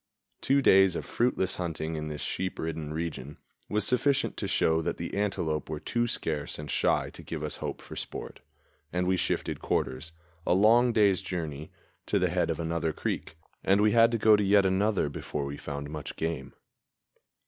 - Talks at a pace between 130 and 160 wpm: No, average, 190 wpm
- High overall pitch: No, very low, 85 Hz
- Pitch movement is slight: No, average, 5.0 semitones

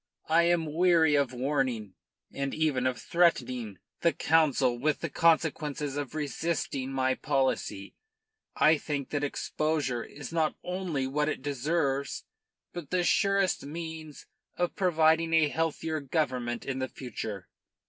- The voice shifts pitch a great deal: No, average, 3.6 semitones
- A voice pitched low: No, medium, 150 Hz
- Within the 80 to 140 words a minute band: Yes, slow, 135 wpm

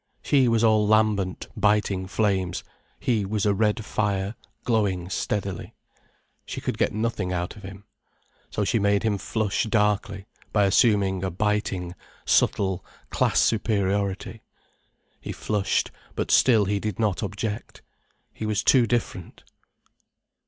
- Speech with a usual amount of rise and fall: No, narrow, 2.0 semitones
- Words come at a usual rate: No, slow, 130 wpm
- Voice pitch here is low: Yes, low, 105 Hz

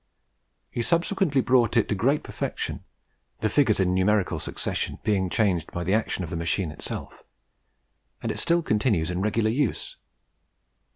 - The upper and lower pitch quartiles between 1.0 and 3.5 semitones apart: No, wide, 5.4 semitones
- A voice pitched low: Yes, low, 105 Hz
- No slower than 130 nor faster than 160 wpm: Yes, average, 155 wpm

